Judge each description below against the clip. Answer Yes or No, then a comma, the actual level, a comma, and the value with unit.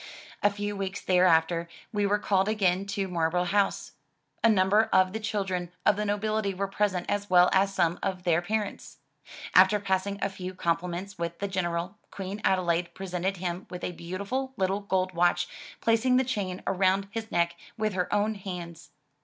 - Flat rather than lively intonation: Yes, narrow, 2.3 semitones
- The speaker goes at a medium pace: Yes, average, 175 wpm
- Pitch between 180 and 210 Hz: Yes, high, 190 Hz